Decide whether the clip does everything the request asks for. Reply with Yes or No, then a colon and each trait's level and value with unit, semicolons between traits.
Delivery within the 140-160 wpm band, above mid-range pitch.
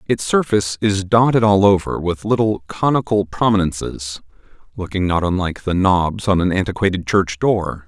No: average, 150 wpm; low, 100 Hz